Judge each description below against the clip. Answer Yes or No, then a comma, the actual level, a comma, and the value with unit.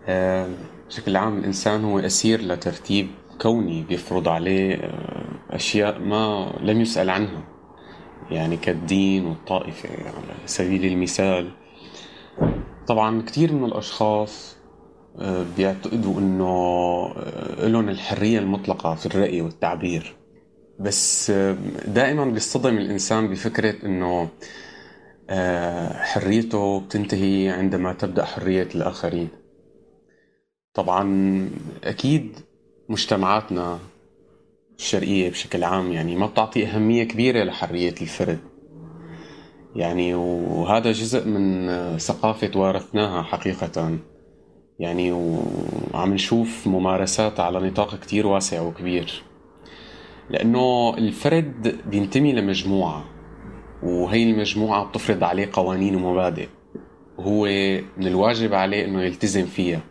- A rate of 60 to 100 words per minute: Yes, average, 90 wpm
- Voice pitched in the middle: No, very low, 95 Hz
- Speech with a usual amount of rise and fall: Yes, average, 3.3 semitones